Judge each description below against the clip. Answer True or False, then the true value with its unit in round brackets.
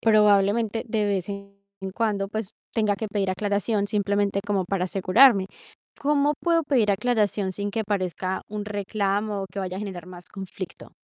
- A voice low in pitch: False (205 Hz)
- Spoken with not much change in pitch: True (1.9 semitones)